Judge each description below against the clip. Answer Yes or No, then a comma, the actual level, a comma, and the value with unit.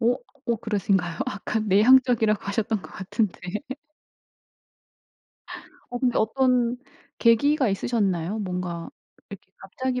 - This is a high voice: Yes, high, 220 Hz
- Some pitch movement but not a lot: Yes, average, 4.1 semitones